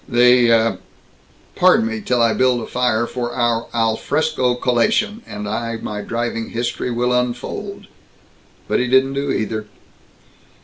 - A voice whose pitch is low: Yes, low, 120 Hz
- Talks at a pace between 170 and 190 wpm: No, average, 140 wpm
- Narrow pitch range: Yes, narrow, 1.6 semitones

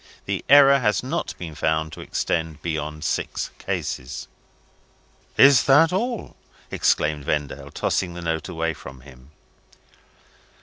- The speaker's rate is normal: No, slow, 125 wpm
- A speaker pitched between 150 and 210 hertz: No, very low, 80 Hz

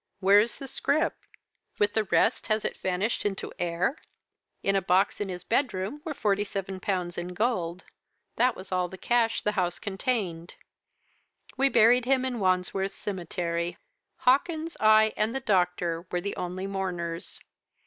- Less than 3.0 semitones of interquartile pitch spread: No, average, 4.3 semitones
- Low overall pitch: No, high, 195 Hz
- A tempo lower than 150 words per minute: No, average, 160 wpm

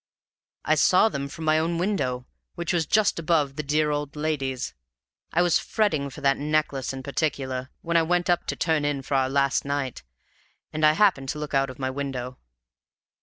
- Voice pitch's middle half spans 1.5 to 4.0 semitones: Yes, average, 3.0 semitones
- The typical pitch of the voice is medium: Yes, medium, 150 Hz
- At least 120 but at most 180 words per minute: No, average, 195 wpm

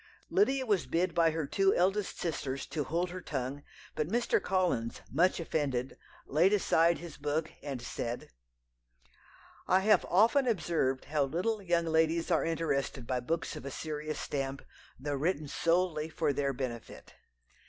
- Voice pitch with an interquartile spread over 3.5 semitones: Yes, average, 4.6 semitones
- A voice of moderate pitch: Yes, medium, 160 Hz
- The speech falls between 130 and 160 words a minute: Yes, average, 155 wpm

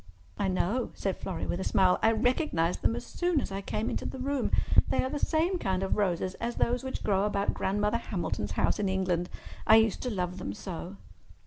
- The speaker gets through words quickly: Yes, fast, 215 wpm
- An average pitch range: Yes, average, 4.9 semitones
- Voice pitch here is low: No, high, 200 Hz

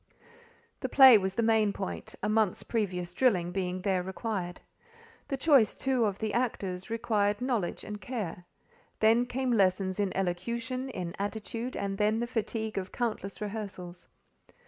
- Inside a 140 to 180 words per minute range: Yes, average, 150 wpm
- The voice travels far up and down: No, average, 3.7 semitones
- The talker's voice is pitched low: No, high, 210 Hz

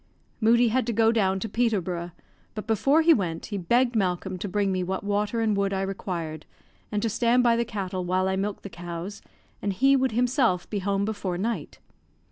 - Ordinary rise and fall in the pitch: Yes, average, 3.8 semitones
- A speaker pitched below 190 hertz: No, high, 205 Hz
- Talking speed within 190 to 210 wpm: Yes, fast, 205 wpm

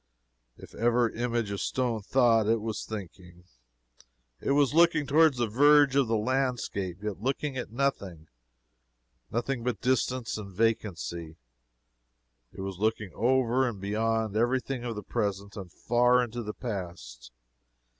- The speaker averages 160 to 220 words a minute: No, average, 145 wpm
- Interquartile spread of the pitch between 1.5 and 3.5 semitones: No, average, 4.1 semitones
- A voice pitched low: Yes, low, 115 Hz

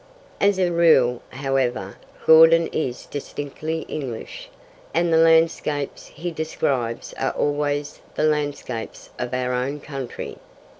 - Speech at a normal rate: No, slow, 115 wpm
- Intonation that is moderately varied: Yes, average, 4.0 semitones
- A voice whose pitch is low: No, medium, 145 Hz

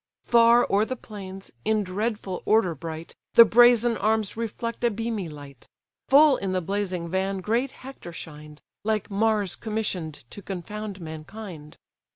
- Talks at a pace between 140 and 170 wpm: Yes, average, 145 wpm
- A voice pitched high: Yes, high, 205 Hz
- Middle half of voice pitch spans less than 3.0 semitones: No, average, 4.2 semitones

